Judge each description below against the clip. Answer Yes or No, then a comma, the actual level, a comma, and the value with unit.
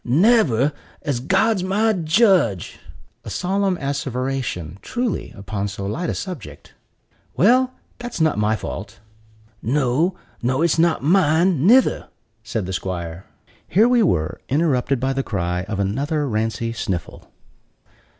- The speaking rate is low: Yes, slow, 130 wpm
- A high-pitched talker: No, medium, 140 Hz